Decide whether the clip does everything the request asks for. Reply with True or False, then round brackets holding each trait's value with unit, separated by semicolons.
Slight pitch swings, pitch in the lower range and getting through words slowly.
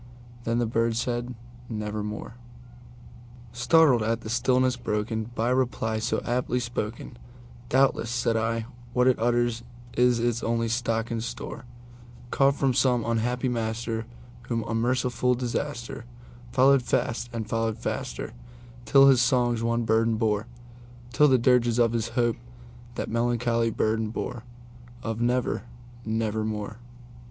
True (1.2 semitones; 120 Hz; 115 wpm)